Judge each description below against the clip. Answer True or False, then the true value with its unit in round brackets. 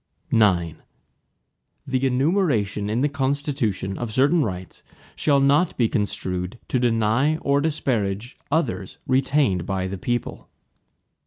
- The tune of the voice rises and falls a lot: True (6.1 semitones)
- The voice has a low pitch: True (120 Hz)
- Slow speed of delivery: True (115 wpm)